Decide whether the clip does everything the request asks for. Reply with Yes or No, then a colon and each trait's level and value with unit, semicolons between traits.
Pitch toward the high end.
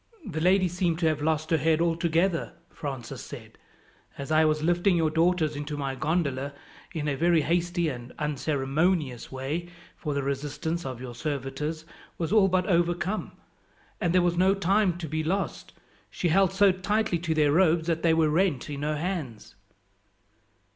No: medium, 160 Hz